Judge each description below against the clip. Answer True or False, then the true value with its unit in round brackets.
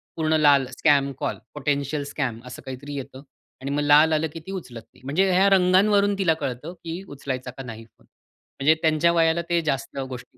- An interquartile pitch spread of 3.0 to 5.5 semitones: True (3.8 semitones)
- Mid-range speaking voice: True (150 Hz)